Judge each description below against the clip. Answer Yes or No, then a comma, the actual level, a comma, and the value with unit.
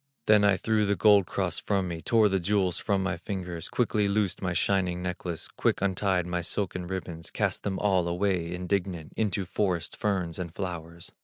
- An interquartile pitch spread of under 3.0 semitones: Yes, narrow, 2.5 semitones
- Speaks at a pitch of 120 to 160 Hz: No, very low, 95 Hz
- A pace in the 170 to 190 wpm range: Yes, average, 180 wpm